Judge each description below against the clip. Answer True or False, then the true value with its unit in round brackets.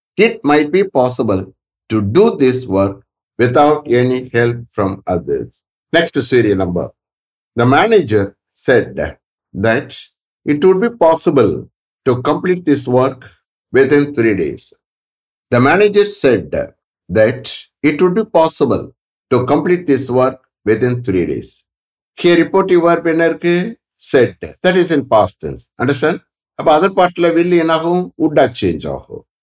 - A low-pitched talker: False (150 Hz)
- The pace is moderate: False (120 wpm)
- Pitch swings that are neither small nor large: False (6.0 semitones)